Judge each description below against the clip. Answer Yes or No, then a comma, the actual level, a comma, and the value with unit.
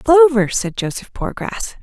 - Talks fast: No, slow, 130 wpm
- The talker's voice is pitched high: Yes, high, 235 Hz